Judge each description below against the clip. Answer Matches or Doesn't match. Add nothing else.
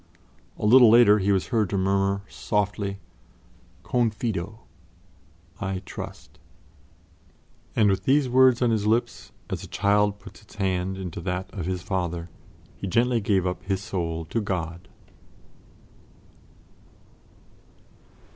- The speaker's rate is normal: Doesn't match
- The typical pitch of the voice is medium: Doesn't match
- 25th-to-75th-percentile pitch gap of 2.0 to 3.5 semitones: Matches